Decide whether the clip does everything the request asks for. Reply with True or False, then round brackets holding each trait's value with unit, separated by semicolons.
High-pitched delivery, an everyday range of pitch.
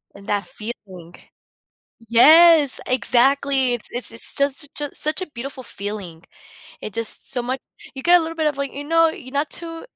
True (265 Hz; 4.8 semitones)